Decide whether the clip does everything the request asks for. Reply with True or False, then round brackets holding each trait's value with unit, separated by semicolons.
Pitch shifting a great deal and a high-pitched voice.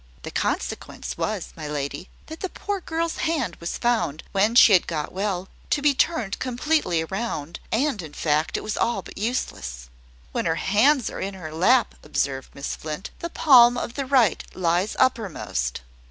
True (8.2 semitones; 205 Hz)